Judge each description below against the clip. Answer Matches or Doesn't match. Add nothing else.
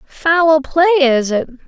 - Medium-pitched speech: Doesn't match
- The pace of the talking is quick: Doesn't match